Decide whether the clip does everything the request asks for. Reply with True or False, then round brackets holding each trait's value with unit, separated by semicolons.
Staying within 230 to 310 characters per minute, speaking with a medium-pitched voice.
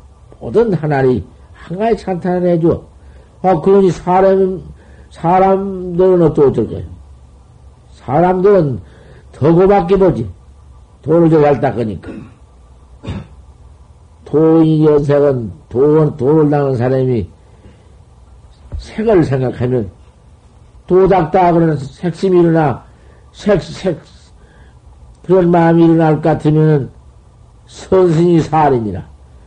False (200 characters per minute; 145 Hz)